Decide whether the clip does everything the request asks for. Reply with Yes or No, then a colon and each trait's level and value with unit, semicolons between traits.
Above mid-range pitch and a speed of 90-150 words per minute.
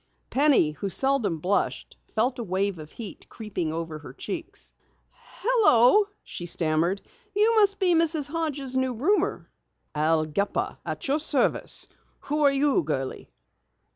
Yes: very high, 250 Hz; average, 140 wpm